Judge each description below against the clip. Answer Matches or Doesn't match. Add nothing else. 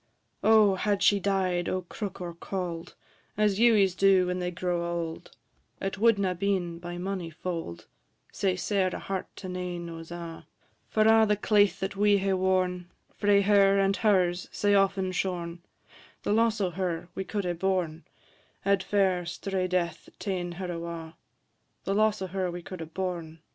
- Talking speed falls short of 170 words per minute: Doesn't match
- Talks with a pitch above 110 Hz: Matches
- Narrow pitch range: Matches